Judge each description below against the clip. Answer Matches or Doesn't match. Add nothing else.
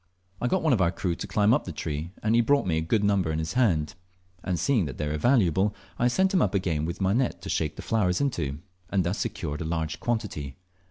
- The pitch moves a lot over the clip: Matches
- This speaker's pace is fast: Matches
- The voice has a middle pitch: Doesn't match